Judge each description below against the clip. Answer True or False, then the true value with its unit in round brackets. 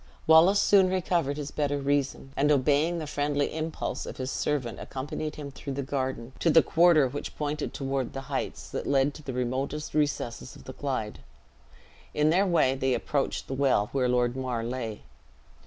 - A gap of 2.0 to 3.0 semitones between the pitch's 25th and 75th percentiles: True (2.6 semitones)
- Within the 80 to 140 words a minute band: False (180 wpm)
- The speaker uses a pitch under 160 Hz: True (140 Hz)